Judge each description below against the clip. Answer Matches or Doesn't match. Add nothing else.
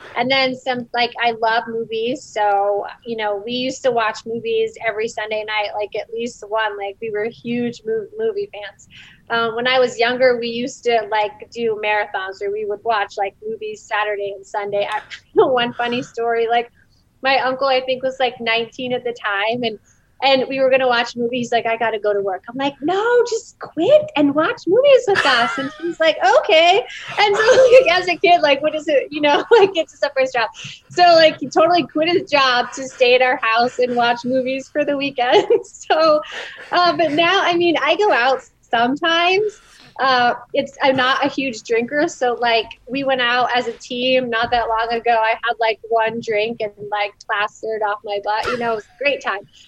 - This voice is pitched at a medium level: Doesn't match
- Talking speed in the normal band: Doesn't match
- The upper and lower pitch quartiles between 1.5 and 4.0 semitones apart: Doesn't match